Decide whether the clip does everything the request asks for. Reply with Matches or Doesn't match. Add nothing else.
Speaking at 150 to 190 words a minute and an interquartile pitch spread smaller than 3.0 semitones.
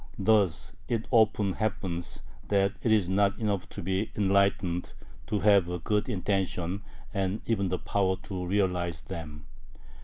Doesn't match